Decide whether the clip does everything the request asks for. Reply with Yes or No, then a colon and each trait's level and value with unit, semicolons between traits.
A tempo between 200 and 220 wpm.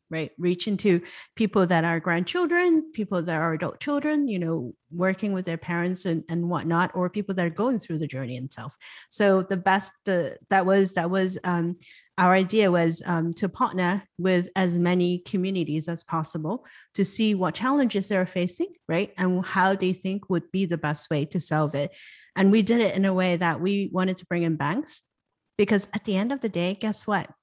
Yes: fast, 205 wpm